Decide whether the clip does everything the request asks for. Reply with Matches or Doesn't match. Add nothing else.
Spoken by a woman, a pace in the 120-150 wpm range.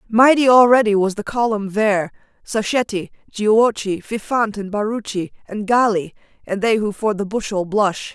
Matches